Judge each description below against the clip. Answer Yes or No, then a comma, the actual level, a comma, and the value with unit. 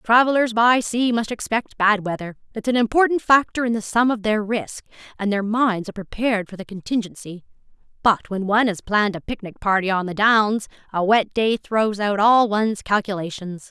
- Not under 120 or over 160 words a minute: No, average, 195 wpm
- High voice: Yes, high, 215 Hz